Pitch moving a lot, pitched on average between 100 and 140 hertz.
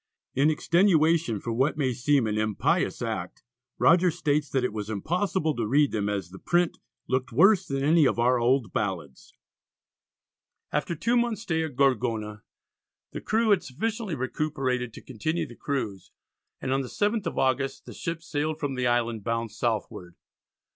Yes: wide, 6.0 semitones; low, 135 Hz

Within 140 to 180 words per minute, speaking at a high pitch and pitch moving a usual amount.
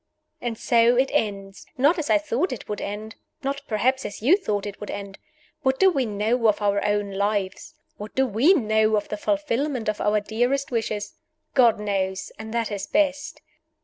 No: average, 190 wpm; high, 220 Hz; average, 4.3 semitones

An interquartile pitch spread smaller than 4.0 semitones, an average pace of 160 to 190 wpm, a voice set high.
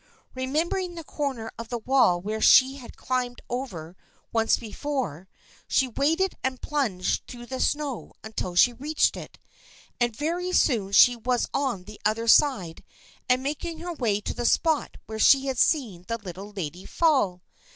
No: average, 5.0 semitones; average, 165 wpm; high, 245 Hz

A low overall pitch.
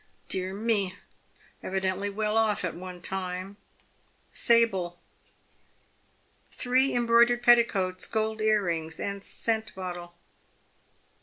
No: high, 200 Hz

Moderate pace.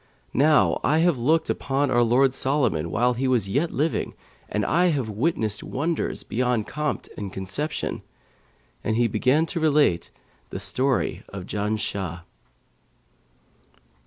No: slow, 130 wpm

